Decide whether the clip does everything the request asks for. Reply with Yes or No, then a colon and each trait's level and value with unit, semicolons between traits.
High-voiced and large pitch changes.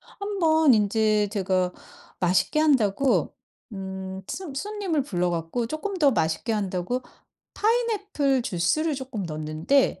Yes: high, 230 Hz; wide, 8.6 semitones